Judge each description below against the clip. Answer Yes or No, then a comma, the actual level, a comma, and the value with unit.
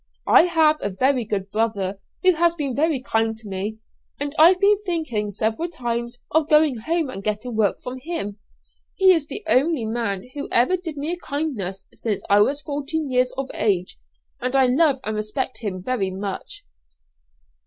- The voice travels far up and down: Yes, wide, 6.6 semitones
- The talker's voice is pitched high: Yes, very high, 255 Hz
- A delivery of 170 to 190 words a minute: Yes, average, 180 wpm